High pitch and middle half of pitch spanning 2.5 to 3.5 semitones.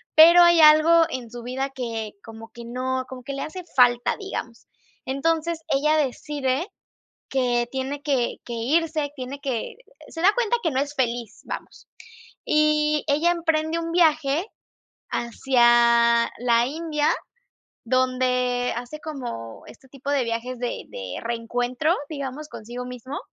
No: very high, 265 Hz; average, 4.0 semitones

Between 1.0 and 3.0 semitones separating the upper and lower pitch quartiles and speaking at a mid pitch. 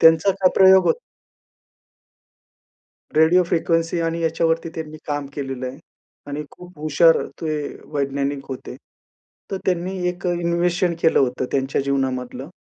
No: average, 3.8 semitones; medium, 160 Hz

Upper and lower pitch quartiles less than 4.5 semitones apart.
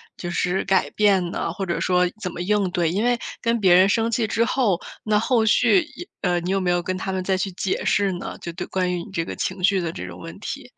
Yes: average, 3.0 semitones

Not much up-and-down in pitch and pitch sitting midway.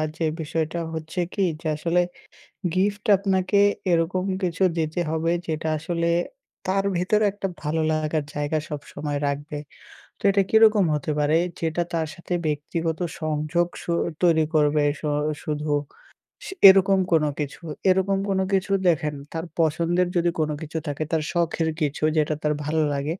No: average, 3.0 semitones; medium, 160 Hz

